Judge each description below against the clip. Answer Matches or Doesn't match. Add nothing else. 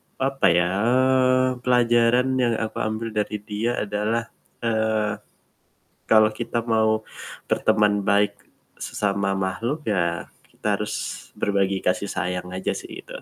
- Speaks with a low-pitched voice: Matches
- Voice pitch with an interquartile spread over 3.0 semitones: Doesn't match